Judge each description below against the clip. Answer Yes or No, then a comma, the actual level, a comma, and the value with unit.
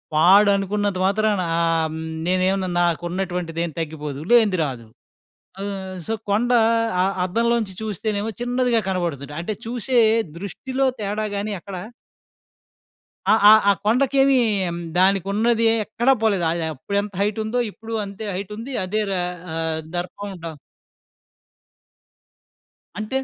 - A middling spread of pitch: Yes, average, 3.9 semitones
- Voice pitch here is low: No, high, 200 Hz